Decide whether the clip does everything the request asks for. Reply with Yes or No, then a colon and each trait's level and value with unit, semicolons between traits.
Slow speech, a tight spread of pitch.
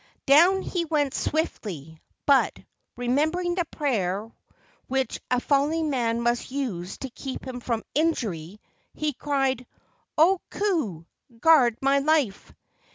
No: slow, 120 wpm; average, 5.0 semitones